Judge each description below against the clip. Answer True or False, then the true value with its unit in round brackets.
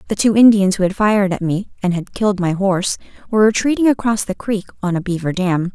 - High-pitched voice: True (200 Hz)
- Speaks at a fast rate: True (230 wpm)